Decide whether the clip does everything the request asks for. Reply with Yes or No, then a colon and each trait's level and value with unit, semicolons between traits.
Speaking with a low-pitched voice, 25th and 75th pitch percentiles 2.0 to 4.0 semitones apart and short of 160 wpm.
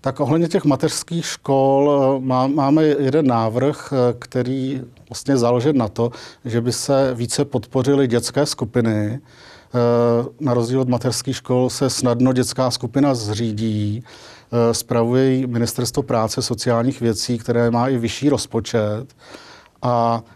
Yes: low, 125 Hz; narrow, 2.5 semitones; average, 120 wpm